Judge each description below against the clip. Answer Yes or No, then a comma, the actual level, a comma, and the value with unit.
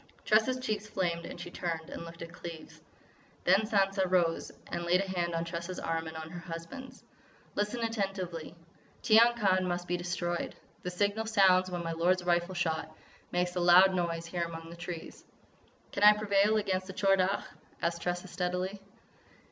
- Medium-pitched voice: Yes, medium, 180 Hz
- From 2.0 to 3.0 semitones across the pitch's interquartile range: Yes, narrow, 2.4 semitones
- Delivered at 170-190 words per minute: Yes, average, 175 wpm